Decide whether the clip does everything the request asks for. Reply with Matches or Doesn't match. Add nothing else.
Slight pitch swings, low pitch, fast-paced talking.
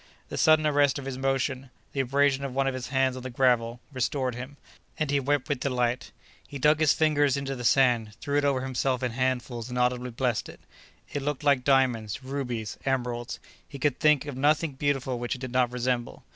Matches